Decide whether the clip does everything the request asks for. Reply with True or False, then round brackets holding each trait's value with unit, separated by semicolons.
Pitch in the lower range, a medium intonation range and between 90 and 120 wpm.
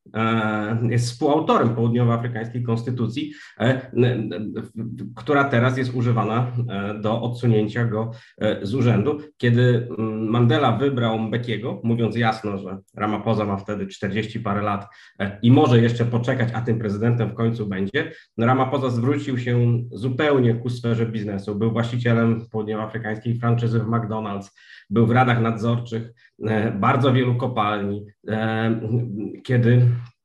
False (115 Hz; 1.9 semitones; 115 wpm)